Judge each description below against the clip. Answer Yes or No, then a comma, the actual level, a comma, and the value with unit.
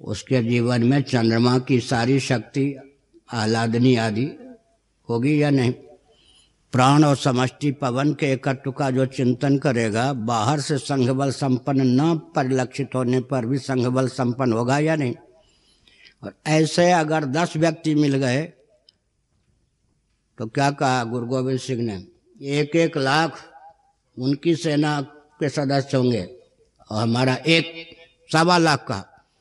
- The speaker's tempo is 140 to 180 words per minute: No, average, 130 wpm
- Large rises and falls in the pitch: No, average, 3.1 semitones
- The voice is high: No, low, 135 Hz